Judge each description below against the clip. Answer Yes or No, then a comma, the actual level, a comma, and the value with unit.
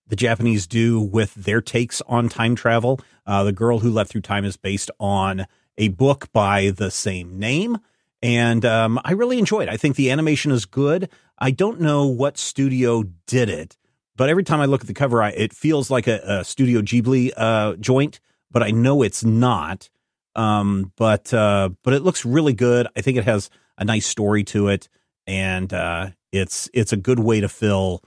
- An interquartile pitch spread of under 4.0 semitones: No, average, 4.4 semitones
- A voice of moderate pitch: No, low, 115 Hz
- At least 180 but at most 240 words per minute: Yes, average, 200 wpm